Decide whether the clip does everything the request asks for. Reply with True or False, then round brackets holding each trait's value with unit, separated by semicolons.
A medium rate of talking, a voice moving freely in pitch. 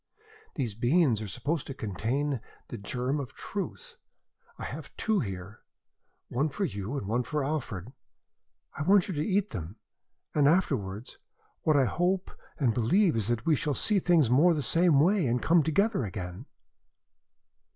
True (160 wpm; 7.1 semitones)